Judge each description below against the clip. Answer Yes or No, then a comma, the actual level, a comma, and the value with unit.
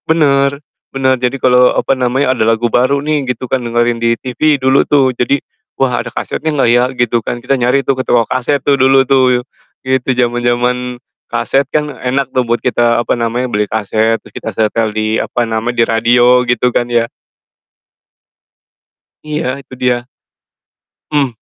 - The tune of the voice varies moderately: No, narrow, 2.1 semitones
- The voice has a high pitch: No, low, 125 Hz